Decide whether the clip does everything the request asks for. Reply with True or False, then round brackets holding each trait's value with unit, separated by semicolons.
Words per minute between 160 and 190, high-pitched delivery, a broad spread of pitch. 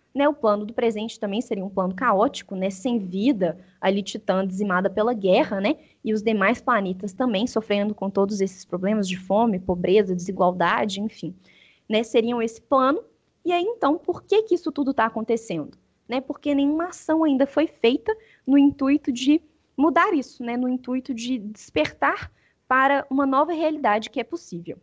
True (175 wpm; 230 Hz; 6.0 semitones)